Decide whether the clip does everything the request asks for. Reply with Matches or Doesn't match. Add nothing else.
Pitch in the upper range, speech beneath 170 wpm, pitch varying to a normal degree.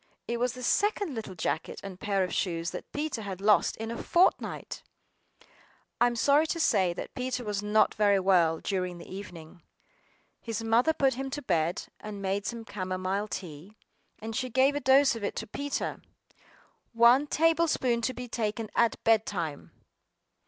Doesn't match